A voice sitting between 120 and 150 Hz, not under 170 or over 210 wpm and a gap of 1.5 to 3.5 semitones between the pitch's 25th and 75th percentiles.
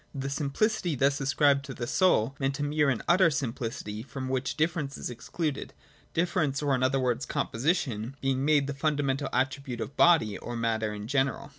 Yes: low, 135 Hz; average, 185 wpm; average, 2.7 semitones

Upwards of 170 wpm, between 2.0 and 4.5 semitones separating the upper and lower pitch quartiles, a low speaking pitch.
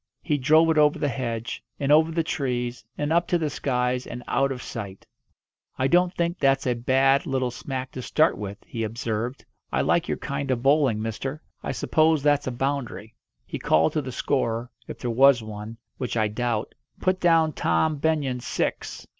Yes: average, 190 wpm; average, 3.8 semitones; low, 130 Hz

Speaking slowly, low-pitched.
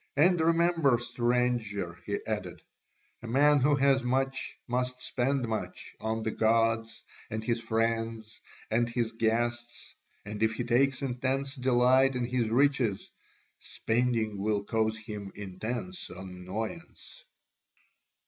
Yes: slow, 120 wpm; low, 120 Hz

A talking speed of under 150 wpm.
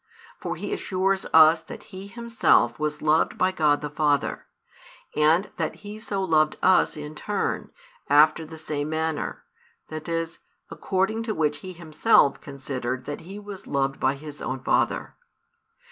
No: average, 155 wpm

